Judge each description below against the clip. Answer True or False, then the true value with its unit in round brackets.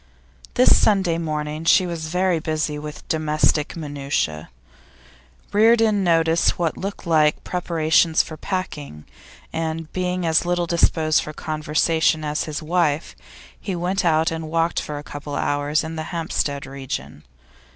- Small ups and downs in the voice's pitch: True (2.3 semitones)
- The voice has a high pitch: False (160 Hz)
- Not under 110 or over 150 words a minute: True (140 wpm)